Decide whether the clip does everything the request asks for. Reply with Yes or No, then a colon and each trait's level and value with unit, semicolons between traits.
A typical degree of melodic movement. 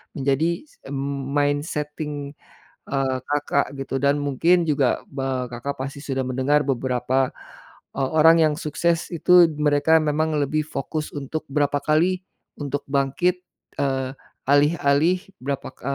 No: narrow, 2.1 semitones